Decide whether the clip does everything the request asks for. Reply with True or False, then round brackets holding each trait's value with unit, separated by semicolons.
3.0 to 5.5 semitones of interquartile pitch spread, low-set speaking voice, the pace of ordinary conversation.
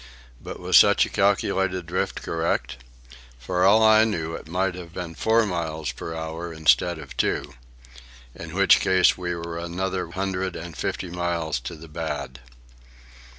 False (2.4 semitones; 85 Hz; 150 wpm)